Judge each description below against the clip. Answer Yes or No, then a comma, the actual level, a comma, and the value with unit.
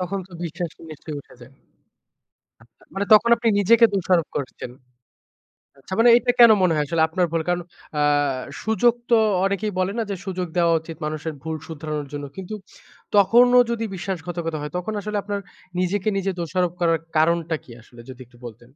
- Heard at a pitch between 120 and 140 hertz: No, medium, 175 Hz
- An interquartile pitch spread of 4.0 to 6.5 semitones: Yes, average, 4.3 semitones